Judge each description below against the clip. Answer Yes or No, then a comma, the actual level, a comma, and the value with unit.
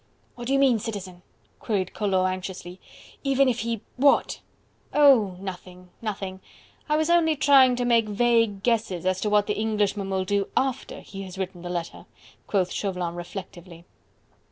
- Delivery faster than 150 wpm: Yes, average, 160 wpm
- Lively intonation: No, average, 4.4 semitones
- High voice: Yes, high, 205 Hz